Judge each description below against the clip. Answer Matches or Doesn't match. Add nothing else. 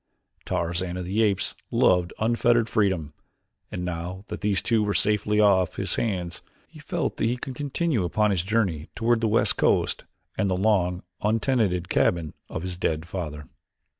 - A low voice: Matches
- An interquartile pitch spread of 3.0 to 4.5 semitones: Matches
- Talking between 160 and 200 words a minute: Matches